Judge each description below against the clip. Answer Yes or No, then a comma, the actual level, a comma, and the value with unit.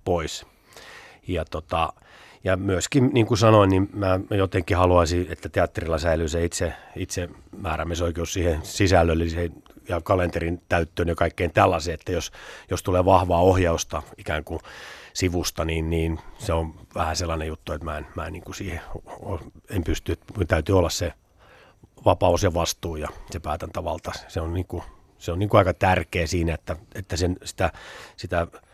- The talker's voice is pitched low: Yes, very low, 90 Hz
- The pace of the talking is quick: Yes, fast, 165 wpm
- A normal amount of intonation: No, narrow, 2.3 semitones